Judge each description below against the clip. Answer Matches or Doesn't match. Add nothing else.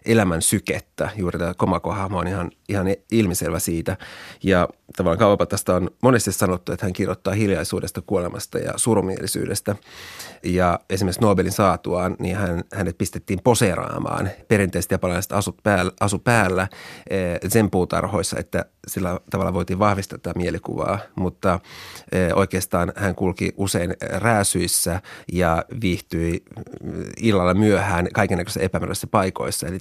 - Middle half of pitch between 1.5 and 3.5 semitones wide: Matches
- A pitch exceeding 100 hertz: Doesn't match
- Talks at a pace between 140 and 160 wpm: Doesn't match